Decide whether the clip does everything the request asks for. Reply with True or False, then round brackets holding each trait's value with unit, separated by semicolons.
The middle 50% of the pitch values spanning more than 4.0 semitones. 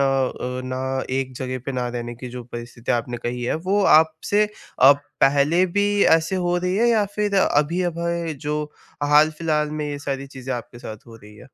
True (4.7 semitones)